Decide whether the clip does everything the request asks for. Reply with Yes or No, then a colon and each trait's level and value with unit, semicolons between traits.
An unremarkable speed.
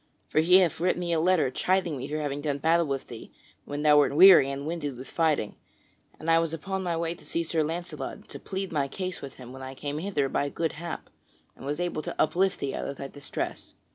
No: fast, 245 wpm